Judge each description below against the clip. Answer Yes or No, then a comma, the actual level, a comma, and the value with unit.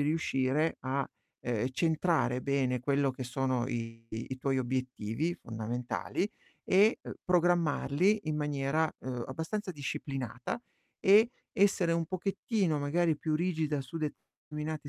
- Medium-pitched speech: Yes, medium, 145 Hz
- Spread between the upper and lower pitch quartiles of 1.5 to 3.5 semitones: No, average, 4.5 semitones